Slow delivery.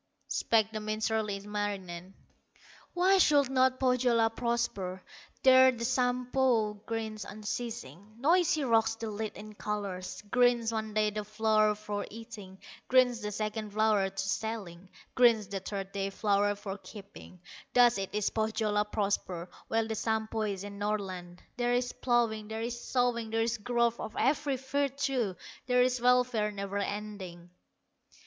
No: average, 145 wpm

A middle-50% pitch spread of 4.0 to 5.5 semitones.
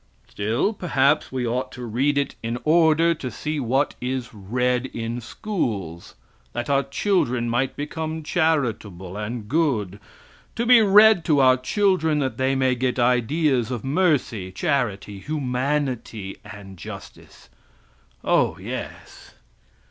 Yes: average, 4.8 semitones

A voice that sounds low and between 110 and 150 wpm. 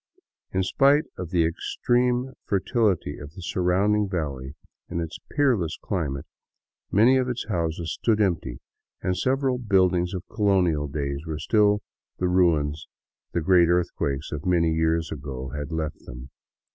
Yes: very low, 90 Hz; average, 145 wpm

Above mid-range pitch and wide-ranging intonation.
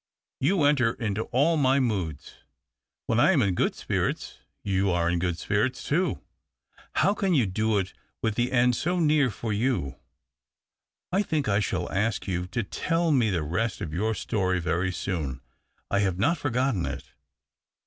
No: low, 110 Hz; wide, 6.6 semitones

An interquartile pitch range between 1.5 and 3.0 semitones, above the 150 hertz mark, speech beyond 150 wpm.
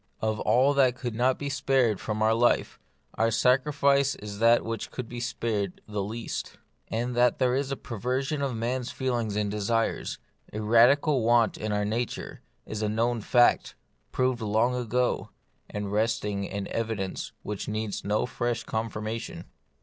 No: average, 2.7 semitones; low, 115 Hz; average, 165 wpm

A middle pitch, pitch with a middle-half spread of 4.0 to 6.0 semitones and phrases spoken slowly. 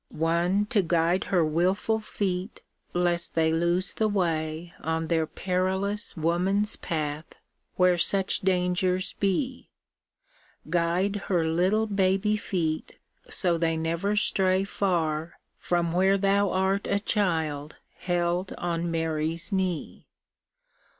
No: medium, 180 Hz; average, 2.8 semitones; slow, 115 wpm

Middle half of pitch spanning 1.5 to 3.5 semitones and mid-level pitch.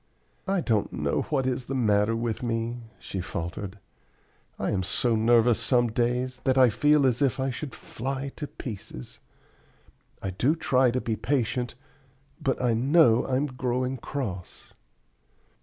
No: average, 2.8 semitones; low, 125 Hz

